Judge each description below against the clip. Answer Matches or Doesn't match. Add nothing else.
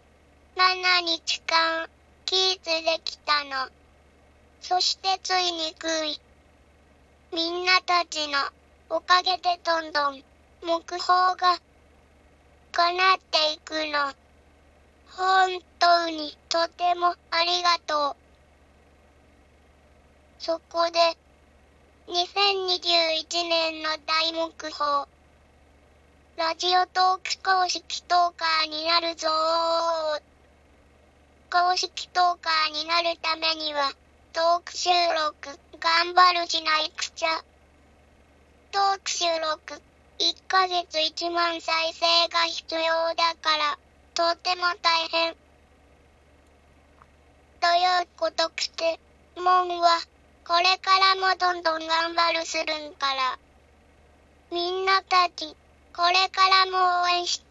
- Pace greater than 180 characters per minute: Doesn't match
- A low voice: Doesn't match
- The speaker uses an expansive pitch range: Doesn't match